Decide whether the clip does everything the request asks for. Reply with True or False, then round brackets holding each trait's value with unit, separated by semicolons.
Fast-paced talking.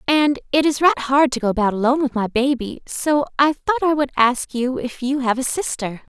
True (235 wpm)